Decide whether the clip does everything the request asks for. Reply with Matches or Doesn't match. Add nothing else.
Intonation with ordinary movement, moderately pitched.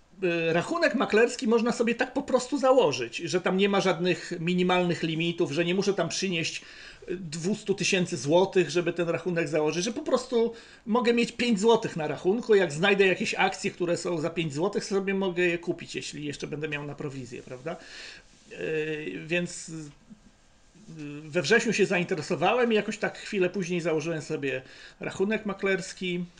Matches